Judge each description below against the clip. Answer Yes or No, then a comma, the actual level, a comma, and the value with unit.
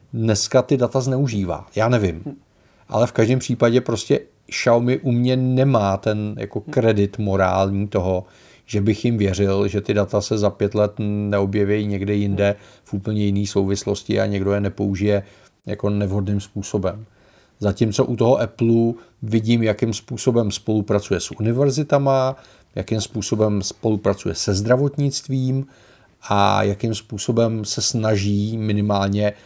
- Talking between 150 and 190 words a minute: No, average, 135 wpm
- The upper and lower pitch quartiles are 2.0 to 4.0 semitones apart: Yes, average, 2.7 semitones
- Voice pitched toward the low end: Yes, low, 105 Hz